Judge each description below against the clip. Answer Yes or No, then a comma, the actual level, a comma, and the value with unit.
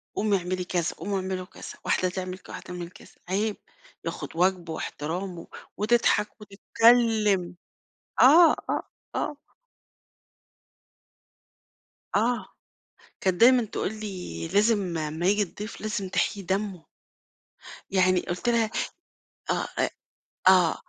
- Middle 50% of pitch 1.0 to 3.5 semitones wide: Yes, average, 3.1 semitones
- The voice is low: No, high, 195 Hz